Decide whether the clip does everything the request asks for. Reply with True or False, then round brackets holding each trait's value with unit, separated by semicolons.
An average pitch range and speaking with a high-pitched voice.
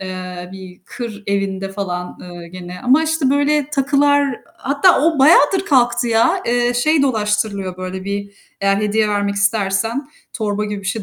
False (6.0 semitones; 210 Hz)